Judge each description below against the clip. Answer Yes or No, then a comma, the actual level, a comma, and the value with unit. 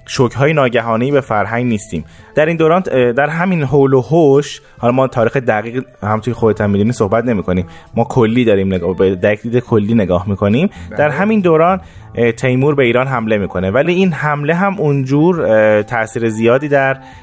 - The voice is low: Yes, low, 120 Hz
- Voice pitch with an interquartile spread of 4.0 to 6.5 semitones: Yes, average, 4.7 semitones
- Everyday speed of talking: No, fast, 170 wpm